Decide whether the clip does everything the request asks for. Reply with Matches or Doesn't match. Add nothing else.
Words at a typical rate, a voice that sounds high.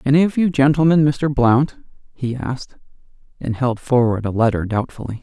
Doesn't match